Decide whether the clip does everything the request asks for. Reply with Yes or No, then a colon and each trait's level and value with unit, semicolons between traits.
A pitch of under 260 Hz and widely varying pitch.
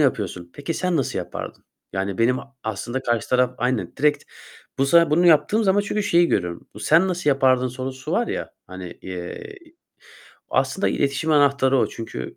Yes: low, 135 Hz; wide, 5.9 semitones